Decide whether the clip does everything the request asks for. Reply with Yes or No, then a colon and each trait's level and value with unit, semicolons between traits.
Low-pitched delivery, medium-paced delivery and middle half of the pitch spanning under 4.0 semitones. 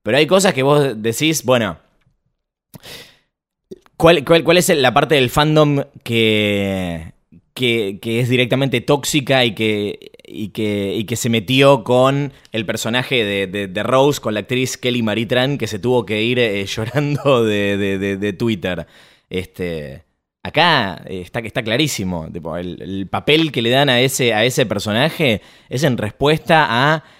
No: low, 120 Hz; average, 165 wpm; average, 5.1 semitones